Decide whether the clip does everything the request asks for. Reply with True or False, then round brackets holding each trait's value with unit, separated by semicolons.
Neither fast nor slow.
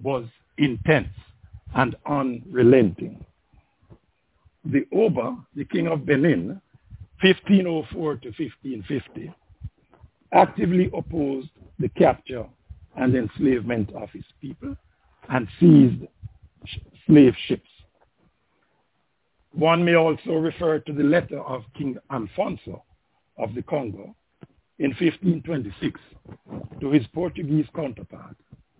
False (95 wpm)